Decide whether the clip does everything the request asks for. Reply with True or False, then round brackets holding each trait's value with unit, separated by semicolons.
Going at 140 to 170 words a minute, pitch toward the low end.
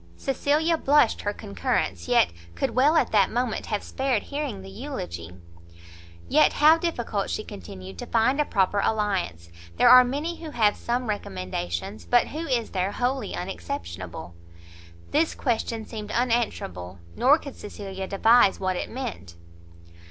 False (145 wpm; 215 Hz)